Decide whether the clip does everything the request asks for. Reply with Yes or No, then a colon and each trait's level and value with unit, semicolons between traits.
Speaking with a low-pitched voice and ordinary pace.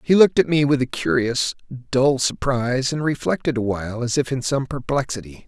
Yes: low, 130 Hz; average, 185 wpm